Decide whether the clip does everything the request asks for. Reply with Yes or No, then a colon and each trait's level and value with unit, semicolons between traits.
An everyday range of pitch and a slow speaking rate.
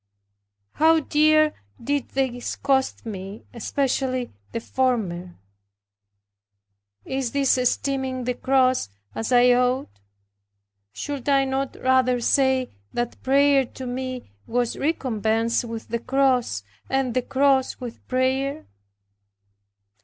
No: narrow, 2.1 semitones; slow, 110 wpm